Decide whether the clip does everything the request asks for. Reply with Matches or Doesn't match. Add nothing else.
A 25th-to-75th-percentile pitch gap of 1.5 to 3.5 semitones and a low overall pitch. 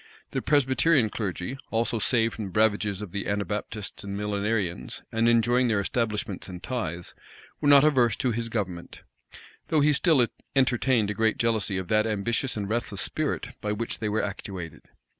Matches